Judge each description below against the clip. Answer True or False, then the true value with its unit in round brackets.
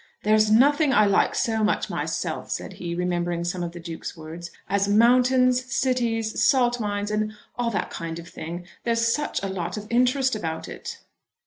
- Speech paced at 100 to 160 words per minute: False (180 wpm)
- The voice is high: True (215 Hz)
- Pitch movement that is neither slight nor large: False (5.7 semitones)